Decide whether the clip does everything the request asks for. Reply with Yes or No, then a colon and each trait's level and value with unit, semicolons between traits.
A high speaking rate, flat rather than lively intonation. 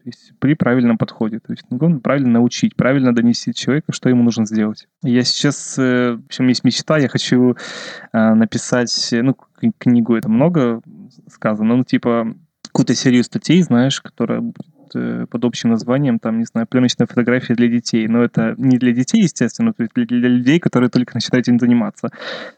Yes: fast, 165 wpm; narrow, 2.0 semitones